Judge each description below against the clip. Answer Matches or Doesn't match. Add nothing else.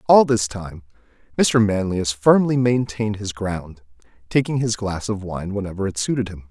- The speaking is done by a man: Matches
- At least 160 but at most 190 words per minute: Matches